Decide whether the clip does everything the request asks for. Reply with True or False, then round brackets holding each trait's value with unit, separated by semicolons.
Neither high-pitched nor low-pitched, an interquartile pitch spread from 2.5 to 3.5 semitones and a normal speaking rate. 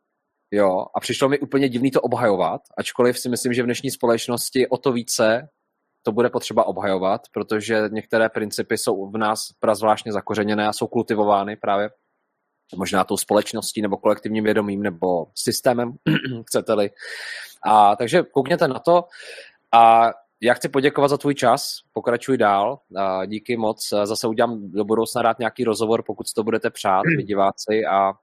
False (115 Hz; 2.9 semitones; 160 wpm)